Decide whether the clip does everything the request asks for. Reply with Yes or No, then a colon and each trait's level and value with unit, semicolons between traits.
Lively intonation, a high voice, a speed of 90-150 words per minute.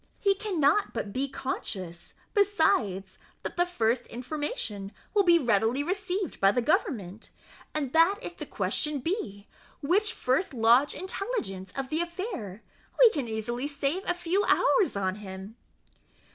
Yes: wide, 9.0 semitones; very high, 280 Hz; average, 145 wpm